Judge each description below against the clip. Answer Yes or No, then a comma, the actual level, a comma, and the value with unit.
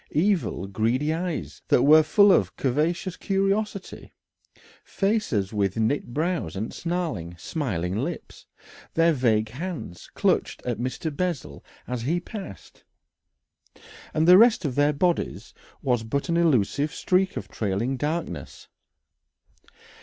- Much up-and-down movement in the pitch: Yes, wide, 7.8 semitones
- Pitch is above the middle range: No, medium, 150 Hz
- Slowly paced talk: Yes, slow, 125 wpm